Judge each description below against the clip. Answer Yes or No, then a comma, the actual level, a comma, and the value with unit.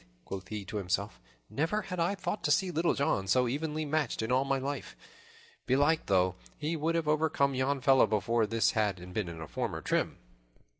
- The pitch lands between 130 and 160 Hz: Yes, low, 135 Hz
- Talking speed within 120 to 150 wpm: No, average, 200 wpm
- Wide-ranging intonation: Yes, wide, 6.7 semitones